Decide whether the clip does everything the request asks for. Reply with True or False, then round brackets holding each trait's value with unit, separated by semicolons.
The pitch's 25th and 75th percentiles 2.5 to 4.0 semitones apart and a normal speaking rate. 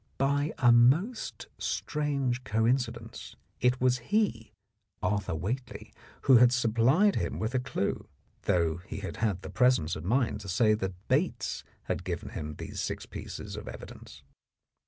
False (4.6 semitones; 155 wpm)